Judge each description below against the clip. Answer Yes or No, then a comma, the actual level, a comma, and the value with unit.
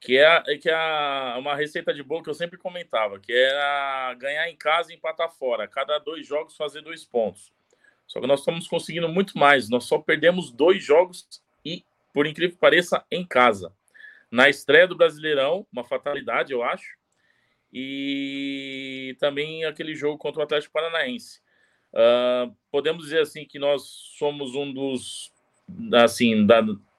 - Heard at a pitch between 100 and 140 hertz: No, medium, 150 Hz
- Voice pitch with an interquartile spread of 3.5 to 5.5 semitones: Yes, average, 3.8 semitones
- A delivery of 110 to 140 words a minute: No, average, 160 wpm